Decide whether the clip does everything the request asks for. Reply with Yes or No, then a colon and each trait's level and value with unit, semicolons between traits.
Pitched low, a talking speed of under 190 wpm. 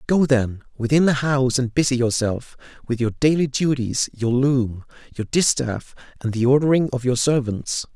Yes: low, 125 Hz; average, 165 wpm